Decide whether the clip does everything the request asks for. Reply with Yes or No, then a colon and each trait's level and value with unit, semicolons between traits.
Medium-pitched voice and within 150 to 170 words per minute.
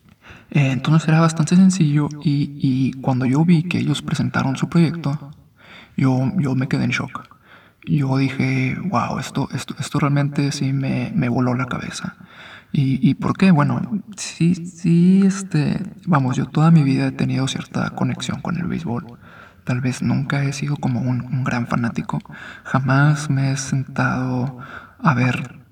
Yes: medium, 145 Hz; average, 160 wpm